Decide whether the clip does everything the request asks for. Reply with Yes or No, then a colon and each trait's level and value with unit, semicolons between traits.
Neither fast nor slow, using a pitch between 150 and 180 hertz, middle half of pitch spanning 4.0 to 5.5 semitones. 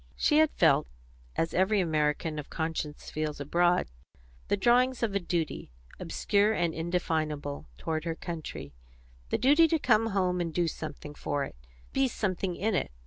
Yes: average, 160 wpm; medium, 175 Hz; average, 5.0 semitones